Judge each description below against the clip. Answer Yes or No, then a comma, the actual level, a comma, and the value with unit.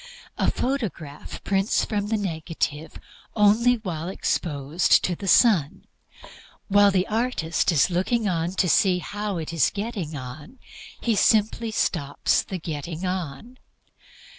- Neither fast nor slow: No, slow, 125 wpm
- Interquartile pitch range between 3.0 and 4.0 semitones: No, average, 4.7 semitones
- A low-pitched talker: No, medium, 185 Hz